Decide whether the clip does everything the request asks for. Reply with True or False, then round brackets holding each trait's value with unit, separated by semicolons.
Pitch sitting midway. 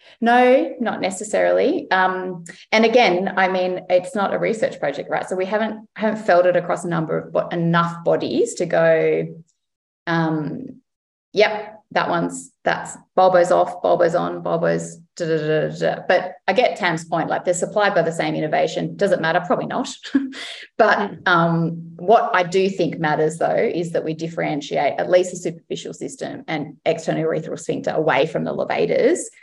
True (180 Hz)